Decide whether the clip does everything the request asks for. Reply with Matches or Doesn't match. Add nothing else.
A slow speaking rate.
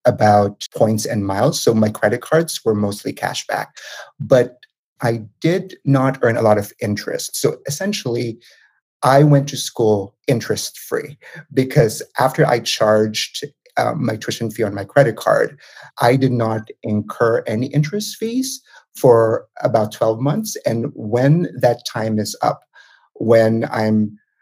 Doesn't match